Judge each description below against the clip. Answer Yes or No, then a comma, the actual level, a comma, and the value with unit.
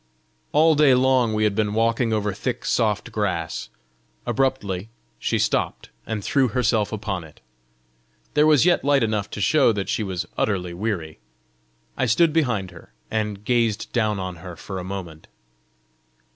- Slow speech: No, average, 160 wpm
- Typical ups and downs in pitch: Yes, average, 4.6 semitones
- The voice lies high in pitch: No, low, 110 Hz